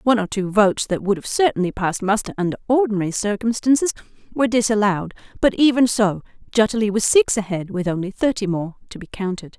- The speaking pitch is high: Yes, high, 210 Hz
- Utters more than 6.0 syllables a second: Yes, 6.4 syllables/s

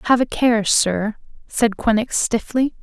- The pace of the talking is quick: No, average, 150 wpm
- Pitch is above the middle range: Yes, high, 225 Hz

